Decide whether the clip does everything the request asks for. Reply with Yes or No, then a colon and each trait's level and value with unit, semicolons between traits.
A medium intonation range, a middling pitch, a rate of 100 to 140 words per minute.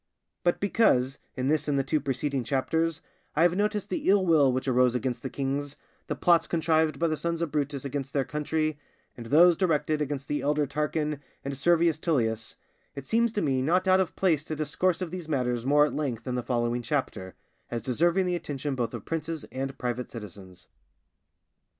No: average, 4.1 semitones; medium, 145 Hz; average, 195 wpm